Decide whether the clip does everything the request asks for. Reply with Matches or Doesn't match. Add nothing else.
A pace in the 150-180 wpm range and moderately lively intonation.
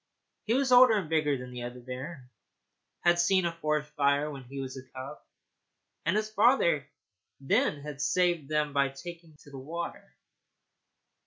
Matches